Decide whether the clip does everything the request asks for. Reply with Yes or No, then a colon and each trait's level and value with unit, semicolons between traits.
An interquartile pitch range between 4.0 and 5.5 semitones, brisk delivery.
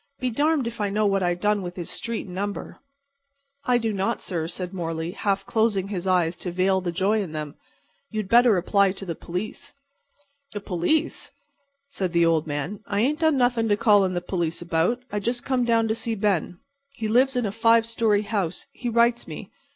Yes: average, 4.3 semitones; fast, 210 wpm